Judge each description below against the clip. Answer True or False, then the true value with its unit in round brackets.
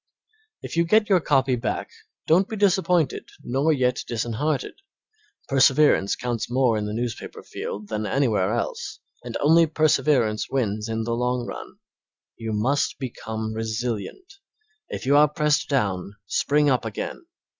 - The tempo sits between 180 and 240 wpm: False (145 wpm)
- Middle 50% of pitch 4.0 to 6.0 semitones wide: True (5.2 semitones)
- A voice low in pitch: True (125 Hz)